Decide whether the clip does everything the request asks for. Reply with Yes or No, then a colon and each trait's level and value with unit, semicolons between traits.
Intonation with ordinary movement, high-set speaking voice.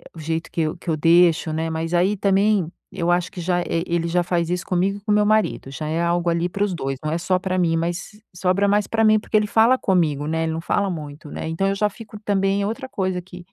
No: average, 3.3 semitones; medium, 180 Hz